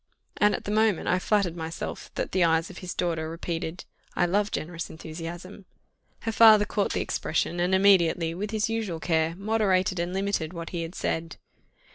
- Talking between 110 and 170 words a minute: No, average, 180 wpm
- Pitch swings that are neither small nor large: Yes, average, 3.4 semitones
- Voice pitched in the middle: Yes, medium, 180 Hz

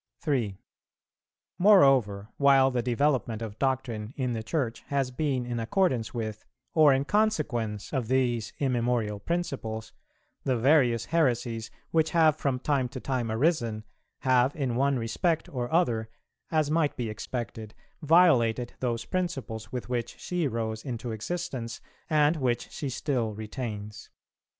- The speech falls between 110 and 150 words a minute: Yes, slow, 135 wpm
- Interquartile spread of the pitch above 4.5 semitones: No, average, 4.2 semitones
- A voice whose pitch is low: Yes, low, 125 Hz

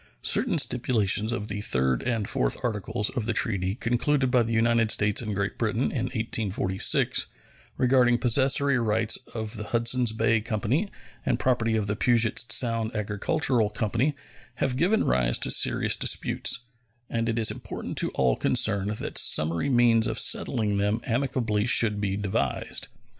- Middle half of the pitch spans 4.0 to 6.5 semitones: No, average, 2.8 semitones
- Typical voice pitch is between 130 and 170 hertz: No, low, 115 Hz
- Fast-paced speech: No, average, 155 wpm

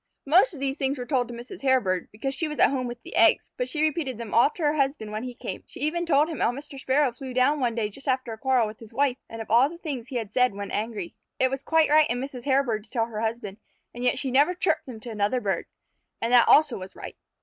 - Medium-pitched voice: No, very high, 255 Hz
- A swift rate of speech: Yes, fast, 280 wpm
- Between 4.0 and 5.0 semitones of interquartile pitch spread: No, average, 3.5 semitones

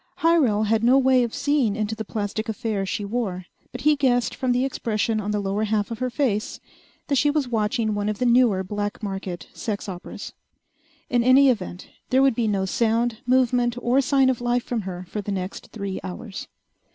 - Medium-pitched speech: No, high, 225 Hz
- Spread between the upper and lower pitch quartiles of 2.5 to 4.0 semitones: Yes, average, 3.4 semitones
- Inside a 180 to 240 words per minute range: Yes, average, 200 wpm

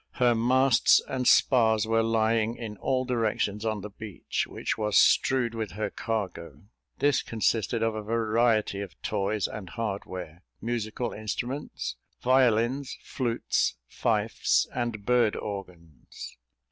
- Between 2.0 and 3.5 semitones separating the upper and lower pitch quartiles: Yes, narrow, 2.4 semitones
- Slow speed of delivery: Yes, slow, 125 wpm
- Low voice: Yes, low, 110 Hz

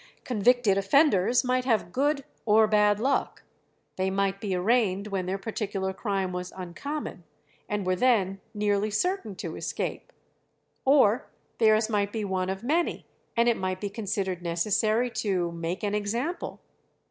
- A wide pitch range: No, average, 3.6 semitones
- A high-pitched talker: Yes, high, 205 Hz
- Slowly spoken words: No, average, 145 wpm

